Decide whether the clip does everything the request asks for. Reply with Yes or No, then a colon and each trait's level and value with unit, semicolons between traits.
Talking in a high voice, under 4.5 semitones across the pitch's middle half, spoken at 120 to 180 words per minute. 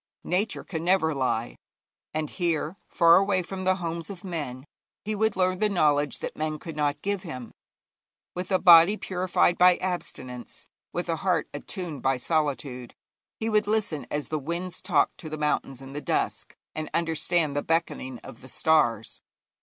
No: medium, 165 Hz; average, 4.0 semitones; average, 170 wpm